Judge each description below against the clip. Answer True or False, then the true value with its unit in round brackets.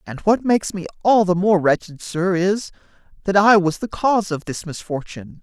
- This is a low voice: False (185 Hz)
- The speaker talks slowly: False (200 wpm)